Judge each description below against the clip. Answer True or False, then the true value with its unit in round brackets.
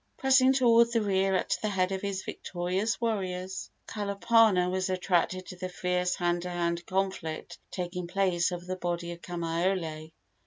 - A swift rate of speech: False (160 wpm)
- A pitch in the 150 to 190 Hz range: True (185 Hz)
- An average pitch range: False (2.1 semitones)